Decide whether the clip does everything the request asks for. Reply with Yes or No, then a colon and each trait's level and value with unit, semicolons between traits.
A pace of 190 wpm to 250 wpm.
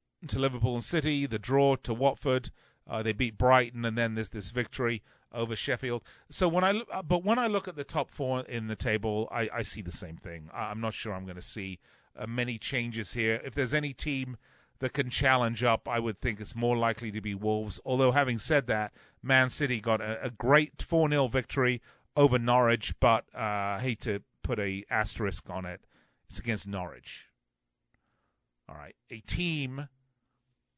Yes: average, 195 wpm